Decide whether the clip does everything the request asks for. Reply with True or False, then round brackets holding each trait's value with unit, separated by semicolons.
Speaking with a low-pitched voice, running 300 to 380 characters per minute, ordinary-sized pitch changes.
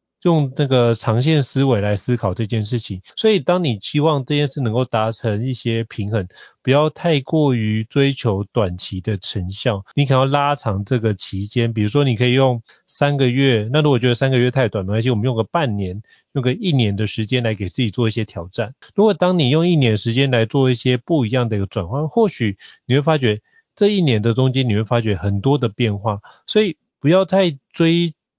True (125 Hz; 310 characters per minute; 4.7 semitones)